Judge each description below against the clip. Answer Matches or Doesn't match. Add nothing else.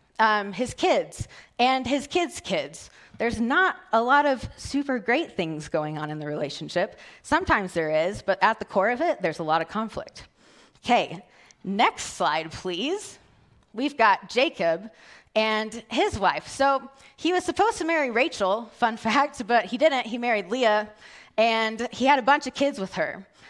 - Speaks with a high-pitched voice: Matches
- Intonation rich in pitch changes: Matches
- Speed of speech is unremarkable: Matches